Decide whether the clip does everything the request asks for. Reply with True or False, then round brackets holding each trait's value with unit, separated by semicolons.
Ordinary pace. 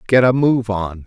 False (225 wpm)